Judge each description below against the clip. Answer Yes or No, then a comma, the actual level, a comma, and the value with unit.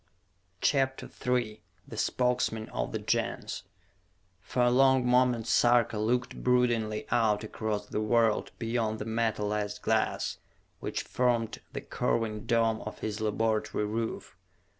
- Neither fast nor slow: No, slow, 125 wpm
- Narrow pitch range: Yes, narrow, 2.3 semitones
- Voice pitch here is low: Yes, low, 115 Hz